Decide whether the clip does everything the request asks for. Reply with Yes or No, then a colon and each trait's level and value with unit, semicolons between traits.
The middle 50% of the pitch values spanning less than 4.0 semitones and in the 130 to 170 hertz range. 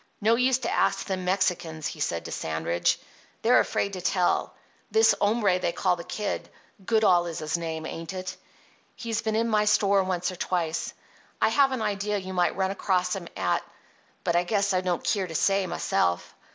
No: average, 3.2 semitones; medium, 185 Hz